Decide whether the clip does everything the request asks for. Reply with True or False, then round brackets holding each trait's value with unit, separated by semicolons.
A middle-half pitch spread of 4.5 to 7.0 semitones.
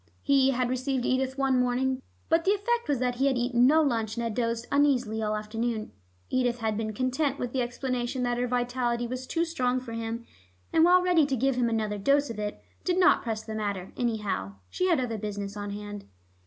False (3.1 semitones)